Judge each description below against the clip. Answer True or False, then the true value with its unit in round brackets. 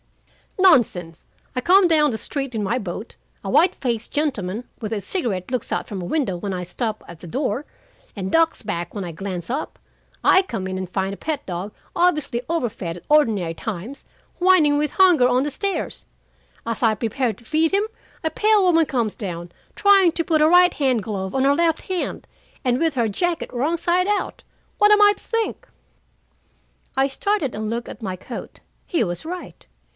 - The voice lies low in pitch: False (255 Hz)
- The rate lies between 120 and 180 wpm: False (195 wpm)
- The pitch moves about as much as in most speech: False (8.6 semitones)